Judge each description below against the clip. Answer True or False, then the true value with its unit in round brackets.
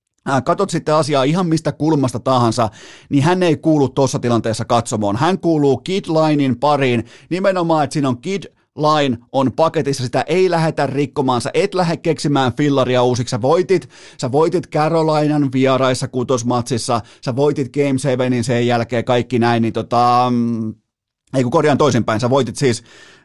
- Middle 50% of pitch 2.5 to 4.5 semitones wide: True (4.1 semitones)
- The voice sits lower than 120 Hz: False (135 Hz)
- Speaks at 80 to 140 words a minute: False (155 wpm)